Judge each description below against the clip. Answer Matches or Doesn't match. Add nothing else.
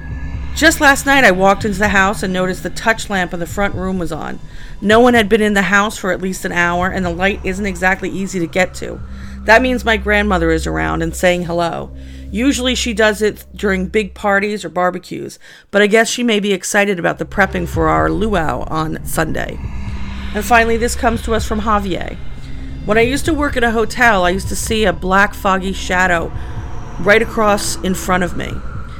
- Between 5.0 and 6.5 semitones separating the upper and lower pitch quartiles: Doesn't match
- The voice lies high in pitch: Matches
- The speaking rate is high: Matches